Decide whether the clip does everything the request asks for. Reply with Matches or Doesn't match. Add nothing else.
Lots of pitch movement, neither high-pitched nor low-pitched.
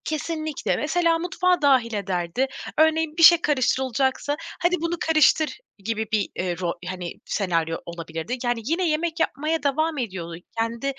Doesn't match